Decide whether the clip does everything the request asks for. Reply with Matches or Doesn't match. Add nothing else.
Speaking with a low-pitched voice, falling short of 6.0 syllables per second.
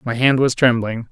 Matches